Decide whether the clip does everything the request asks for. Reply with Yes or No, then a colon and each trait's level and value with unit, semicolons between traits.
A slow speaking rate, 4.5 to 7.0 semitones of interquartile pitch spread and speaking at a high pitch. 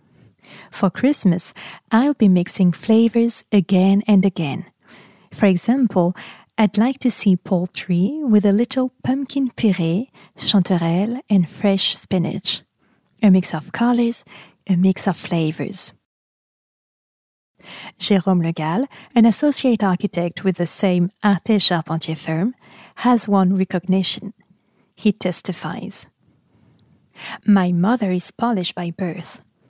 No: slow, 115 wpm; average, 3.9 semitones; high, 195 Hz